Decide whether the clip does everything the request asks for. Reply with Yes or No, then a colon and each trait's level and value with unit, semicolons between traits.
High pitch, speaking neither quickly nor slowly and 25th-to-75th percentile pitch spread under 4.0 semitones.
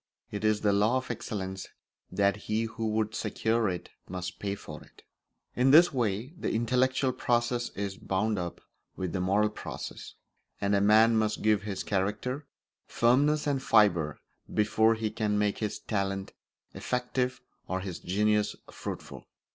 No: low, 105 Hz; average, 155 wpm; average, 3.0 semitones